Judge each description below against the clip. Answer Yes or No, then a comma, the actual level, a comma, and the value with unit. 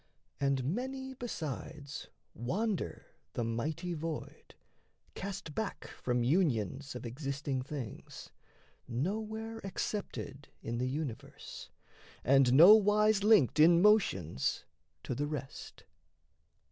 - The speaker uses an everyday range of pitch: No, wide, 7.9 semitones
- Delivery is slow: Yes, slow, 95 wpm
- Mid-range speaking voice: Yes, medium, 150 Hz